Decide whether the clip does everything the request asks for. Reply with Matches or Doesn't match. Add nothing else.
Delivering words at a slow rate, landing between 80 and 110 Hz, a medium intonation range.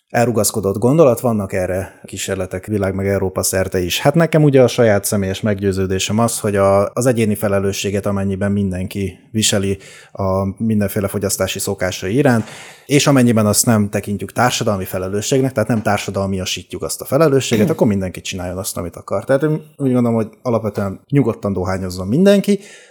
Doesn't match